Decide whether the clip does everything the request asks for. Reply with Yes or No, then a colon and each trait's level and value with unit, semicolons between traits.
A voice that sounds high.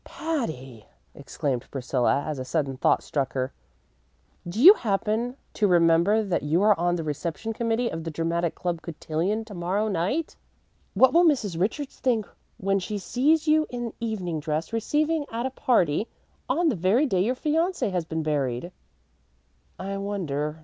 Yes: high, 195 Hz